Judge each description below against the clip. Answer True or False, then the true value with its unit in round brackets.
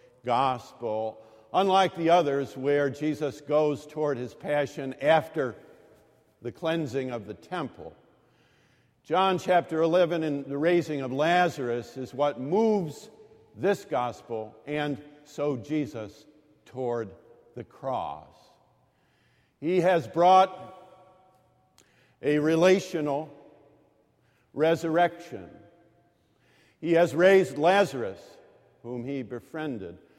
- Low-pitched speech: False (150 Hz)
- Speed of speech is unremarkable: False (95 wpm)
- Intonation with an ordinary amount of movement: True (4.7 semitones)